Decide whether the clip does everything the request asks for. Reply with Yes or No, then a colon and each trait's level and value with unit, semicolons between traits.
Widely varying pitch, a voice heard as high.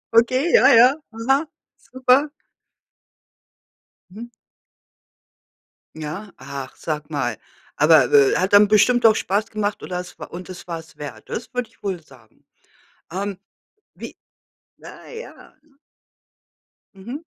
Yes: wide, 7.2 semitones; high, 200 Hz